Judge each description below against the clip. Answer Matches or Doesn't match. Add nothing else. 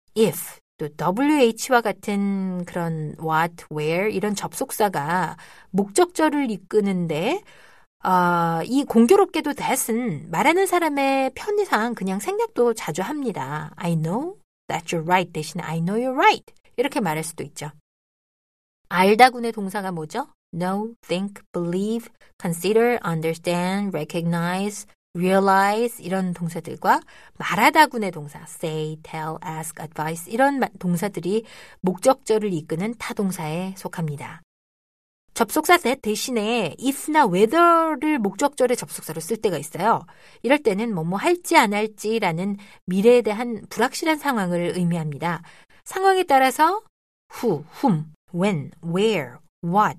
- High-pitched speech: Matches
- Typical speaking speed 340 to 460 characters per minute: Matches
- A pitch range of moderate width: Doesn't match